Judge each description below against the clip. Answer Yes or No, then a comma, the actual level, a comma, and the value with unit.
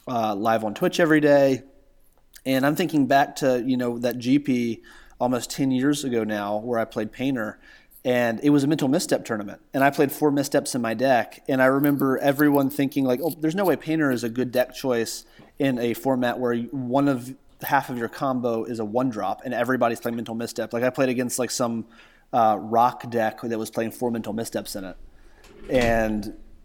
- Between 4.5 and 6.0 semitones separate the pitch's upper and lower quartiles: No, average, 3.0 semitones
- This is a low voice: Yes, low, 125 Hz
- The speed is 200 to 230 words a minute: Yes, fast, 205 wpm